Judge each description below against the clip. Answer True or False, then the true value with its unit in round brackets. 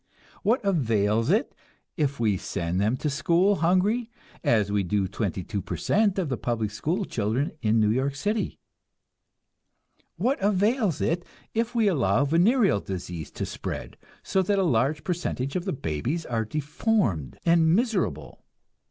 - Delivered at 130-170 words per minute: True (150 wpm)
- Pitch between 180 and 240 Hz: False (145 Hz)